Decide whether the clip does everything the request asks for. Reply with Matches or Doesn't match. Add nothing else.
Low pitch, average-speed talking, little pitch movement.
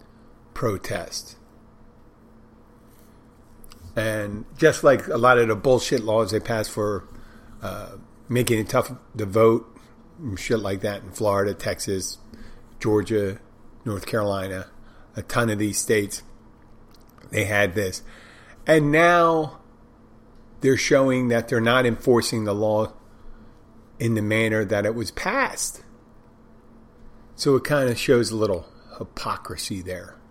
Doesn't match